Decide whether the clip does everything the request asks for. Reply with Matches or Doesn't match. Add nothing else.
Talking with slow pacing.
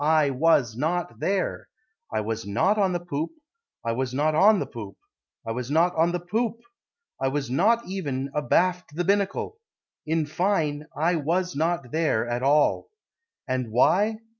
Doesn't match